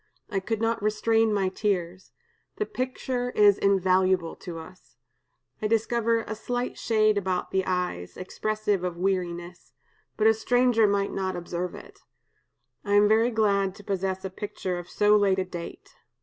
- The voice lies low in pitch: No, high, 200 Hz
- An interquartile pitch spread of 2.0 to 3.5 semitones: Yes, average, 2.9 semitones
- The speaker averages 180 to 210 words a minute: No, average, 160 wpm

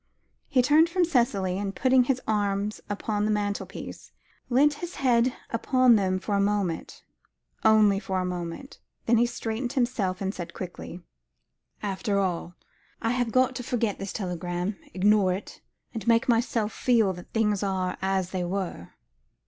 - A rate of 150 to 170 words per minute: Yes, average, 155 wpm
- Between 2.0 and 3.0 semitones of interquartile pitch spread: No, average, 4.2 semitones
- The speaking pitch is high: Yes, high, 210 Hz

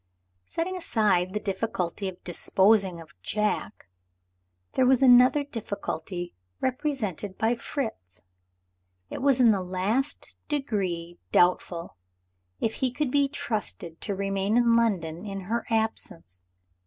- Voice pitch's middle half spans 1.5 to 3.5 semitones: No, wide, 5.4 semitones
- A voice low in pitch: No, high, 210 Hz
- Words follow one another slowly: Yes, slow, 120 wpm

